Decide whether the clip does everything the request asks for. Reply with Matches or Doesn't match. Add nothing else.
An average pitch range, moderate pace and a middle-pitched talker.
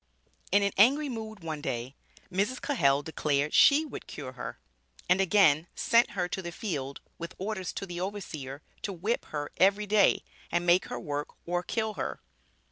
Doesn't match